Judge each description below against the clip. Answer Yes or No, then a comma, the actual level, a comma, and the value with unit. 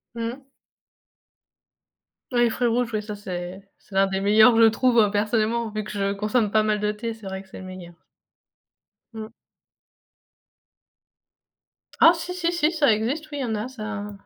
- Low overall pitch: No, high, 215 Hz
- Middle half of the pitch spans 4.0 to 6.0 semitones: No, average, 2.8 semitones